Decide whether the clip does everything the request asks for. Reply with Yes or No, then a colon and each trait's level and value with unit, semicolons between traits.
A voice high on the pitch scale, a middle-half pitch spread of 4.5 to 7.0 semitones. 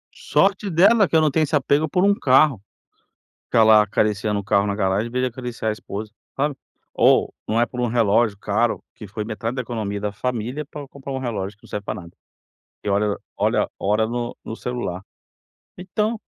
No: low, 115 Hz; average, 4.9 semitones